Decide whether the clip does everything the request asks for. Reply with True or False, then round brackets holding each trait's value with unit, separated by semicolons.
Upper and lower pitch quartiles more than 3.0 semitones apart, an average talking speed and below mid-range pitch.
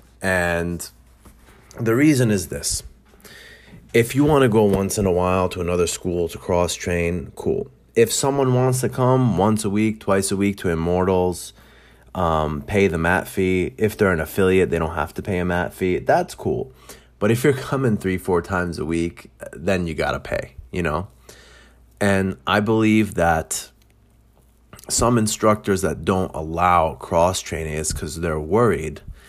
True (4.2 semitones; 170 wpm; 95 Hz)